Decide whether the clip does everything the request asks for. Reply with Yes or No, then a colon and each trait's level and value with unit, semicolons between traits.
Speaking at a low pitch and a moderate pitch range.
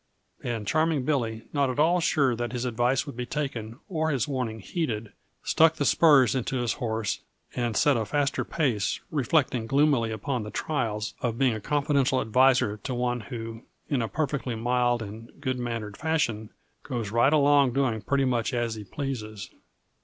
Yes: low, 125 Hz; average, 3.9 semitones